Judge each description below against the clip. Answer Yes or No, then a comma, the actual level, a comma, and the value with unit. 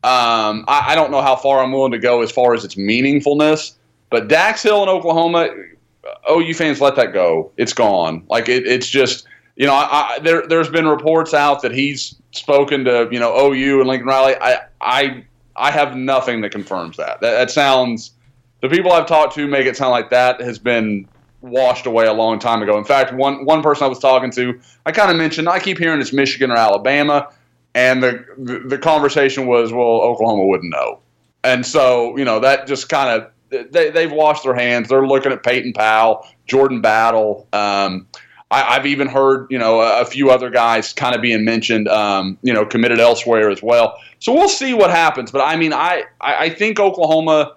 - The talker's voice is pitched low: Yes, low, 130 Hz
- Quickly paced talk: Yes, fast, 210 wpm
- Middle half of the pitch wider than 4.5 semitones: No, average, 3.5 semitones